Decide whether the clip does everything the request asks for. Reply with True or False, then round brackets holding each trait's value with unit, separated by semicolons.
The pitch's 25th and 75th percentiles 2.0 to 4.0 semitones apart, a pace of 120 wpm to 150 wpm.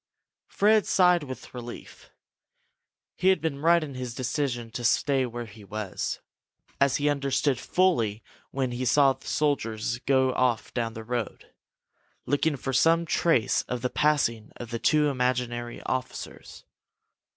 True (3.6 semitones; 145 wpm)